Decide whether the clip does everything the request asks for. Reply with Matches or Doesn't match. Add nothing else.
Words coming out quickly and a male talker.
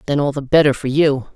Doesn't match